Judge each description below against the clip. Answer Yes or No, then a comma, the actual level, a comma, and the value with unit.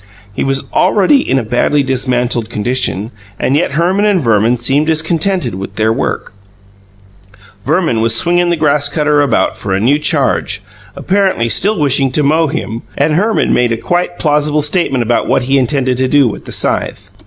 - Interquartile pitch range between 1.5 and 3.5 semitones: No, average, 5.0 semitones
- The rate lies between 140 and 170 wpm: No, average, 180 wpm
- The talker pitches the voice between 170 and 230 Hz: No, medium, 140 Hz